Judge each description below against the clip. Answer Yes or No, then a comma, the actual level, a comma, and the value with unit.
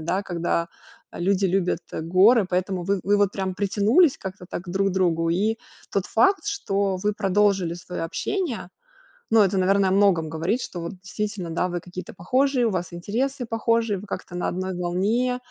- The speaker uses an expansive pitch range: No, average, 2.9 semitones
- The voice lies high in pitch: Yes, high, 195 Hz